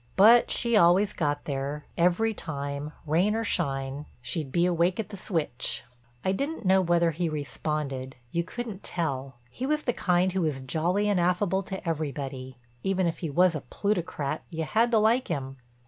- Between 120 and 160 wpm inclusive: No, average, 175 wpm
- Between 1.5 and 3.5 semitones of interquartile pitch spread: No, average, 5.1 semitones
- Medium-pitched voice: Yes, medium, 170 Hz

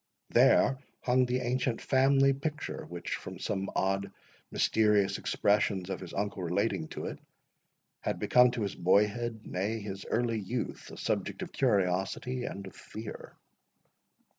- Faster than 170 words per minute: No, average, 140 wpm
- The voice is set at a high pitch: No, low, 105 Hz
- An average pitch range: Yes, average, 4.2 semitones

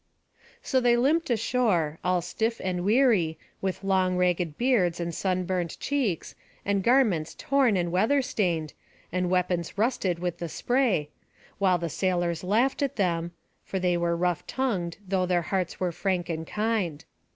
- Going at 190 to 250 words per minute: No, average, 155 wpm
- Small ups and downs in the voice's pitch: No, average, 4.6 semitones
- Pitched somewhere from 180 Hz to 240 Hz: Yes, medium, 185 Hz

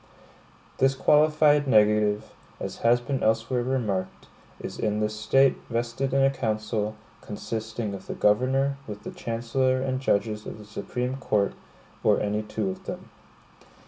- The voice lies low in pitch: Yes, low, 115 Hz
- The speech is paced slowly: No, average, 145 wpm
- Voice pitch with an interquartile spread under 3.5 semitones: No, average, 3.8 semitones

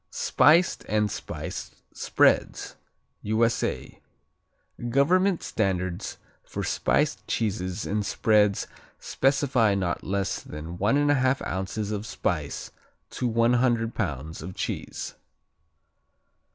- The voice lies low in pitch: Yes, low, 110 Hz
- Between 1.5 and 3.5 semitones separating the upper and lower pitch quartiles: No, average, 5.0 semitones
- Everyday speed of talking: No, slow, 95 wpm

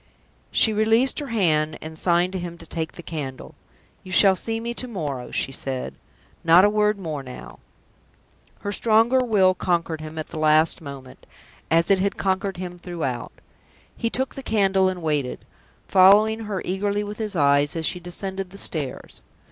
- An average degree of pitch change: Yes, average, 4.8 semitones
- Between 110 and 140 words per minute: No, average, 175 wpm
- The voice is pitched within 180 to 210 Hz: Yes, medium, 185 Hz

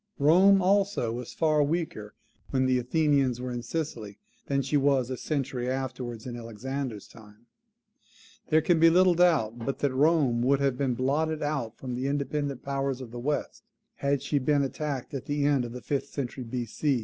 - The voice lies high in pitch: No, low, 135 Hz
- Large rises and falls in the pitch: No, average, 3.3 semitones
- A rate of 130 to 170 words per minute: No, average, 185 wpm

